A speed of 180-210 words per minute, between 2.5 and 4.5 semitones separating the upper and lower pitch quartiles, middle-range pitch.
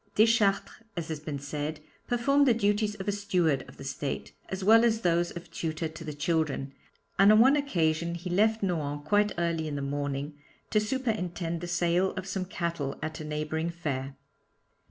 No: average, 185 wpm; average, 5.1 semitones; medium, 170 Hz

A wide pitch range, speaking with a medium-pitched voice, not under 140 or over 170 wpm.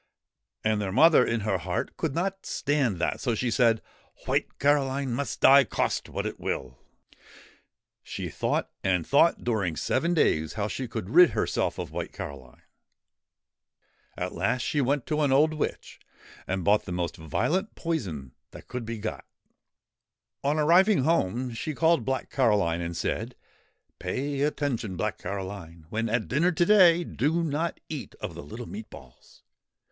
No: wide, 7.7 semitones; low, 125 Hz; average, 165 wpm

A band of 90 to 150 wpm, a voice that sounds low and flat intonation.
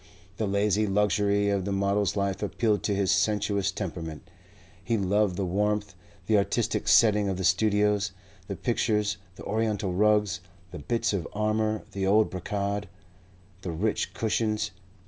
Yes: average, 145 wpm; low, 100 Hz; narrow, 1.5 semitones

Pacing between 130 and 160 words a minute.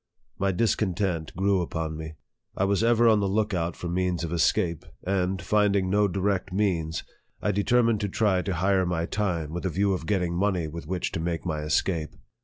No: fast, 205 wpm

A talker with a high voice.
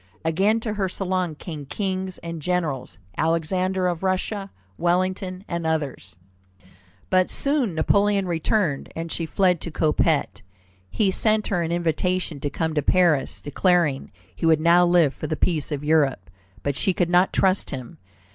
No: medium, 175 Hz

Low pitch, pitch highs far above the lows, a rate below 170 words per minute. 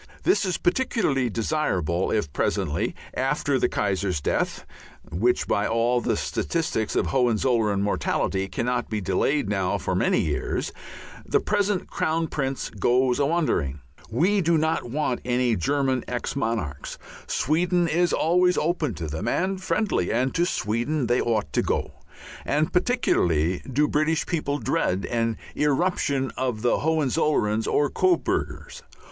Yes: low, 130 Hz; wide, 7.0 semitones; average, 140 wpm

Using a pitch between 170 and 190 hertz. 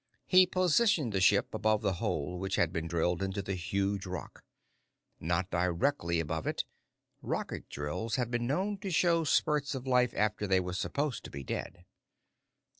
No: low, 100 Hz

